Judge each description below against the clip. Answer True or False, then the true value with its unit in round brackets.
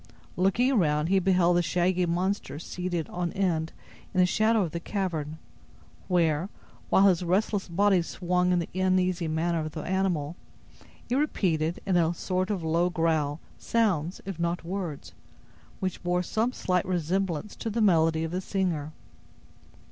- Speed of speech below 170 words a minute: True (155 wpm)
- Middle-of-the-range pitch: True (180 Hz)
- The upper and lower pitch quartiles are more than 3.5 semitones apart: False (2.5 semitones)